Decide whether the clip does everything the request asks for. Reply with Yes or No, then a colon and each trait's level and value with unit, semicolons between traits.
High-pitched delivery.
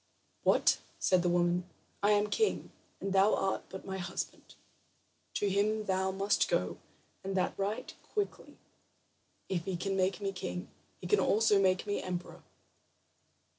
Yes: high, 195 Hz